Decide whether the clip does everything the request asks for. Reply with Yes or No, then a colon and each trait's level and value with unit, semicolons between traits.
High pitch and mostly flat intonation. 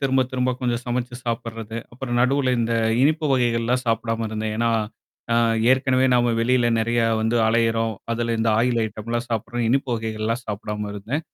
No: low, 115 Hz; narrow, 1.8 semitones